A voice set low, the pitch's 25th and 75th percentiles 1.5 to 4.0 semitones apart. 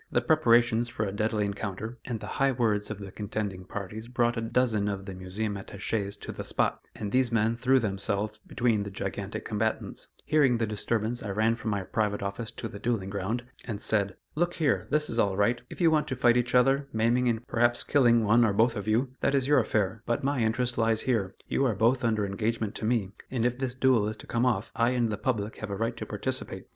Yes: low, 115 Hz; average, 3.0 semitones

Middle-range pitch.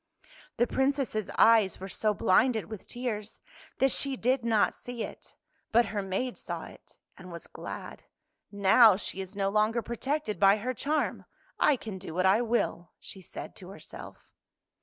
No: high, 215 Hz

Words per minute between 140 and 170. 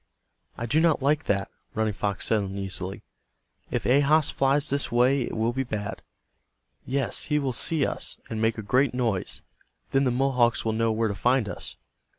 No: average, 180 wpm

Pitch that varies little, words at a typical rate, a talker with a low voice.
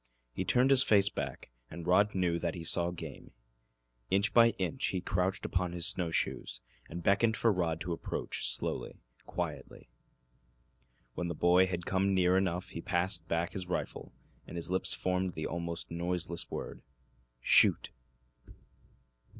Yes: narrow, 2.0 semitones; average, 155 wpm; very low, 90 Hz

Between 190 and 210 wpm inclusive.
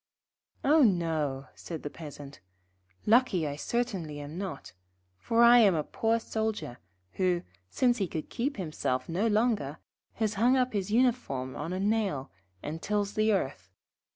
No: average, 155 wpm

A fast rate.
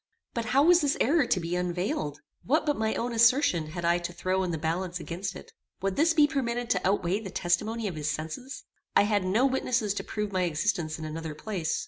Yes: fast, 220 wpm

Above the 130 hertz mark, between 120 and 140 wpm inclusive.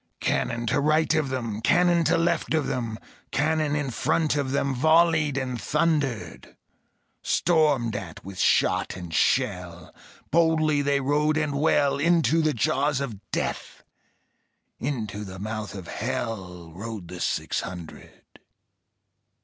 Yes: medium, 140 Hz; slow, 135 wpm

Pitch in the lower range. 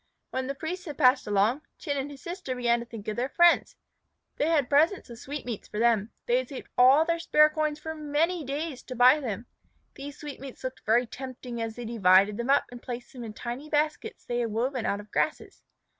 No: very high, 260 Hz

